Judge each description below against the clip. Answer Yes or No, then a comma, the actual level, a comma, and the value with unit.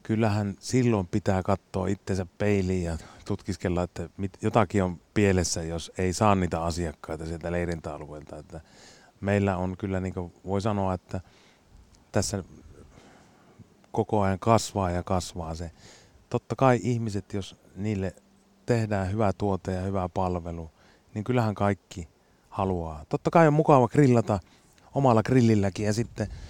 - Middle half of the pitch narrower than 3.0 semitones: No, average, 3.4 semitones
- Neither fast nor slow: Yes, average, 135 wpm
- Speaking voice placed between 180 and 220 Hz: No, very low, 95 Hz